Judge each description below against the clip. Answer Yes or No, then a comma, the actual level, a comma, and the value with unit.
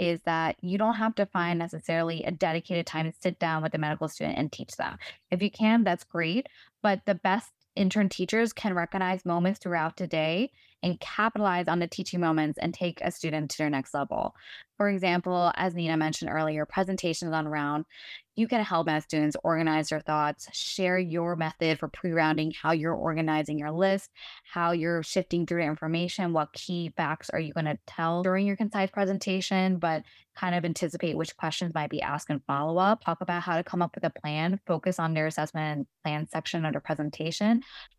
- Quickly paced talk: No, average, 195 wpm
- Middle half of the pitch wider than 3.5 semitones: No, average, 2.9 semitones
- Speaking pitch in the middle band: Yes, medium, 170 Hz